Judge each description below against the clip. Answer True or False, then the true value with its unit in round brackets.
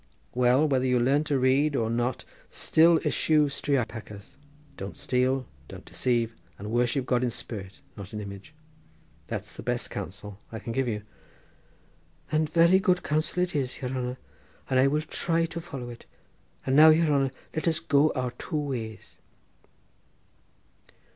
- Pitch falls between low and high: False (130 Hz)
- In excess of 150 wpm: True (160 wpm)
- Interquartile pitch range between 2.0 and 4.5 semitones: True (4.2 semitones)